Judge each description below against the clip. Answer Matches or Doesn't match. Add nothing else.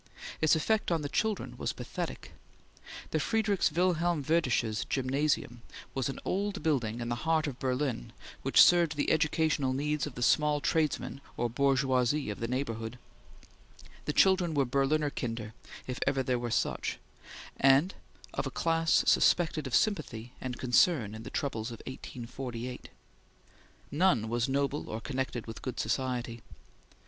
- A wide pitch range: Doesn't match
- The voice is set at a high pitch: Doesn't match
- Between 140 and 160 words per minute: Matches